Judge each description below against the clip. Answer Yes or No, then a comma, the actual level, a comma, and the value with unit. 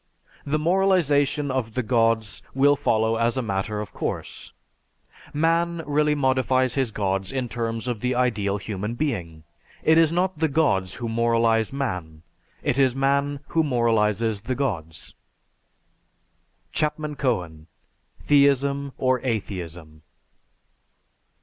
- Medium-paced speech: No, slow, 125 wpm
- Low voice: Yes, low, 125 Hz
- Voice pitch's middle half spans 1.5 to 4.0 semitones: No, average, 4.9 semitones